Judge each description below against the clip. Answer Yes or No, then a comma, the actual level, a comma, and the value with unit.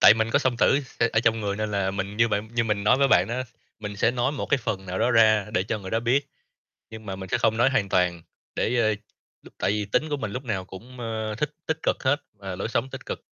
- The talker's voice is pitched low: Yes, low, 110 Hz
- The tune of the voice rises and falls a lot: No, average, 3.5 semitones